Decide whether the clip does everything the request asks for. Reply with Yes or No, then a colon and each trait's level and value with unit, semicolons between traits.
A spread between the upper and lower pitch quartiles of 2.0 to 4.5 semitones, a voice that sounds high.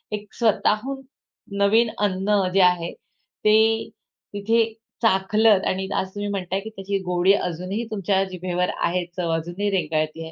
Yes: average, 2.7 semitones; high, 195 Hz